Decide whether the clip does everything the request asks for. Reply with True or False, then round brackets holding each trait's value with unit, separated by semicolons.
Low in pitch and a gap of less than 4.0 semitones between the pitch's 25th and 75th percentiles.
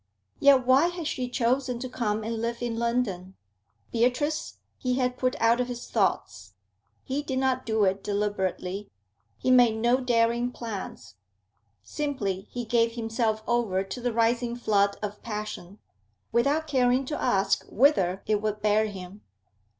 False (235 Hz; 3.3 semitones)